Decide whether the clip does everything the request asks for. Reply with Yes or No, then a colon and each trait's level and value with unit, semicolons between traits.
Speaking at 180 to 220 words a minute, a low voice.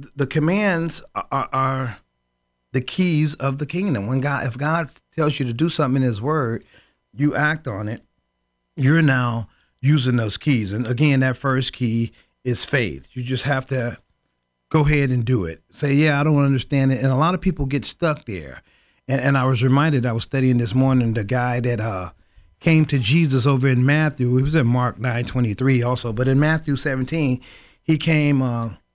Yes: average, 200 wpm; low, 130 Hz